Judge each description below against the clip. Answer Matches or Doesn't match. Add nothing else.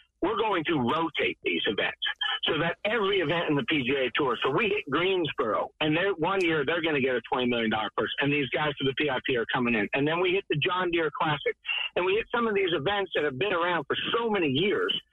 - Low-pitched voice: Doesn't match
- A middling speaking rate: Doesn't match